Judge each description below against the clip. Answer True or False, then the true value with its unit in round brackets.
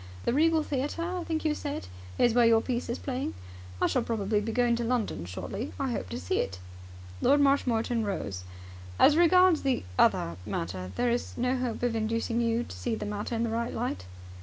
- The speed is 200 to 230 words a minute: True (205 wpm)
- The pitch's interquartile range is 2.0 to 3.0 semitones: False (4.0 semitones)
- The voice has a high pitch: True (235 Hz)